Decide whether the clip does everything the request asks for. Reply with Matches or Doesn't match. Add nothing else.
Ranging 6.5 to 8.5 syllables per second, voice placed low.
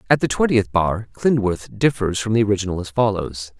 Doesn't match